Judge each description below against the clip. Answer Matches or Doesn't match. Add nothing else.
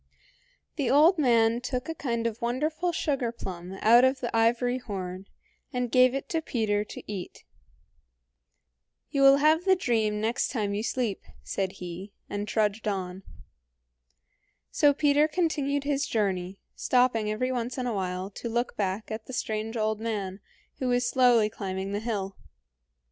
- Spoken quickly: Doesn't match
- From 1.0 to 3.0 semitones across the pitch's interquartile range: Doesn't match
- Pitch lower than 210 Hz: Doesn't match